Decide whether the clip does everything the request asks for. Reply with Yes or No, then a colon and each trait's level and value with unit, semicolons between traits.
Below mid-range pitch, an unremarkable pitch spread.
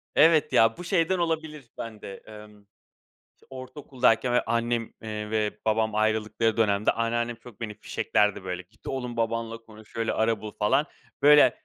Yes: low, 115 Hz; average, 3.0 semitones